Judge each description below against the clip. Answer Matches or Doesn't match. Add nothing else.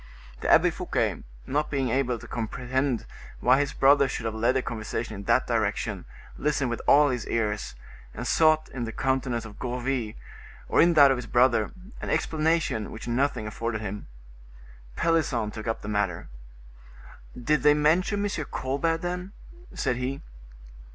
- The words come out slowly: Doesn't match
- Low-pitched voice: Matches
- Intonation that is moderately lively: Matches